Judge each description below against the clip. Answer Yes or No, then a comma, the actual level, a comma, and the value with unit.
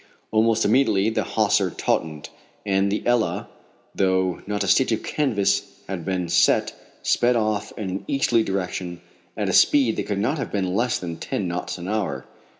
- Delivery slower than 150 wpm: No, average, 175 wpm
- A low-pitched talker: Yes, low, 100 Hz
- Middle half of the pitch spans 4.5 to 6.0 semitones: No, average, 3.3 semitones